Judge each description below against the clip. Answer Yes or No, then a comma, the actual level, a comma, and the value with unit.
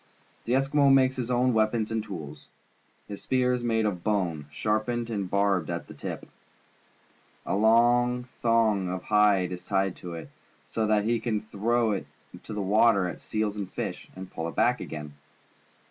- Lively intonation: No, average, 3.8 semitones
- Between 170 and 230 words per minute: Yes, average, 175 wpm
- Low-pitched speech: Yes, low, 110 Hz